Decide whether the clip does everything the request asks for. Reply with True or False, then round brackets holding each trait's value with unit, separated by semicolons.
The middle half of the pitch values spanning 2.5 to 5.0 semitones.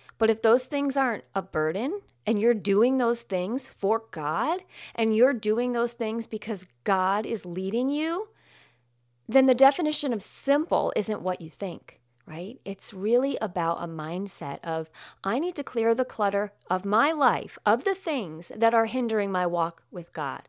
False (5.4 semitones)